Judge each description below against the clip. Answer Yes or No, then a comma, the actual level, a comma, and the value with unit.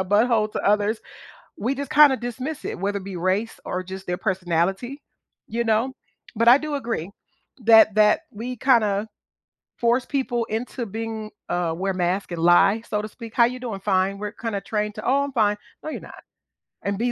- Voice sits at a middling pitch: No, high, 215 Hz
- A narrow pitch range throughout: No, average, 3.6 semitones